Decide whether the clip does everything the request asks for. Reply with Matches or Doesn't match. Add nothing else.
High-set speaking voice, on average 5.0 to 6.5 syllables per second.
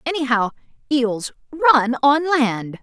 Doesn't match